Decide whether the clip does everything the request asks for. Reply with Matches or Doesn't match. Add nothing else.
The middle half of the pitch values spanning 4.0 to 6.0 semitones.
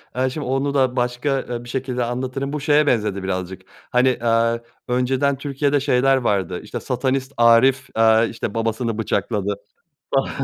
Doesn't match